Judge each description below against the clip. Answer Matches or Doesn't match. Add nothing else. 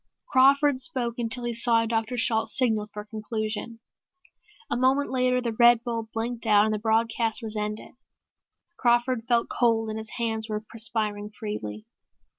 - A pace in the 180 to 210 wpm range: Doesn't match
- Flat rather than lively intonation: Matches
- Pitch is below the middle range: Doesn't match